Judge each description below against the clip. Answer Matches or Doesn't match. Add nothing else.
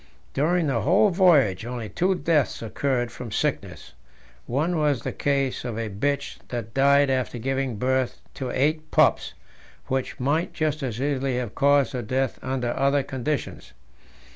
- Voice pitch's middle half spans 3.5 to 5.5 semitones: Doesn't match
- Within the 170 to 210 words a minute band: Doesn't match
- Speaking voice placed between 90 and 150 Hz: Matches